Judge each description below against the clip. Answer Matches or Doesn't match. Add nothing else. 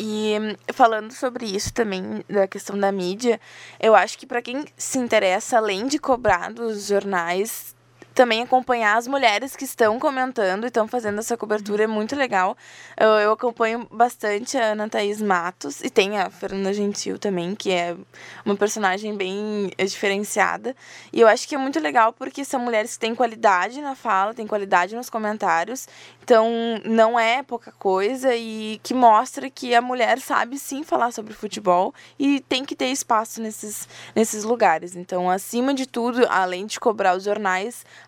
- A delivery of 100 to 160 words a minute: Doesn't match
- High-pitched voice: Matches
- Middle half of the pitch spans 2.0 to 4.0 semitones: Matches